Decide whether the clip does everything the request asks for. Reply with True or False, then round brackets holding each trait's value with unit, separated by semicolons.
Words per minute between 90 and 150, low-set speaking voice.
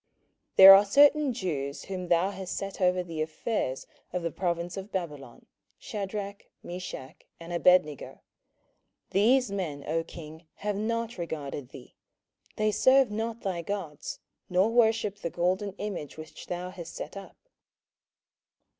False (140 wpm; 185 Hz)